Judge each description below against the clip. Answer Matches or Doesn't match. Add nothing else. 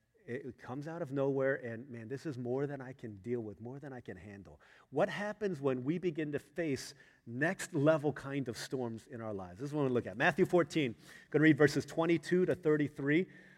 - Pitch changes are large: Doesn't match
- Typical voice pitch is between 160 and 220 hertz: Doesn't match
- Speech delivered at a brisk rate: Matches